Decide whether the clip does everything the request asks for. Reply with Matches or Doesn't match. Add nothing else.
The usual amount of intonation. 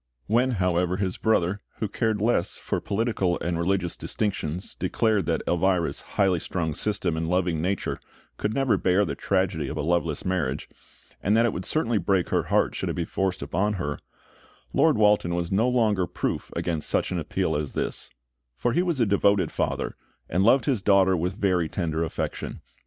Matches